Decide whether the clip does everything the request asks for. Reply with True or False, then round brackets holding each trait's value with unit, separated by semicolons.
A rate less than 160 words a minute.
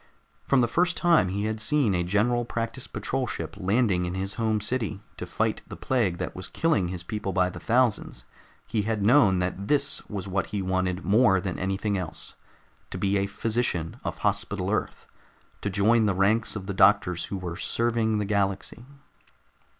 False (185 wpm)